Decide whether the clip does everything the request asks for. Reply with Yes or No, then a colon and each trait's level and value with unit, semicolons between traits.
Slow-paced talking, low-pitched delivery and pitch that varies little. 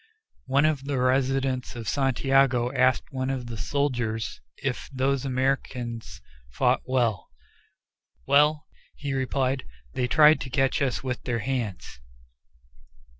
Yes: slow, 125 wpm; low, 130 Hz; narrow, 1.7 semitones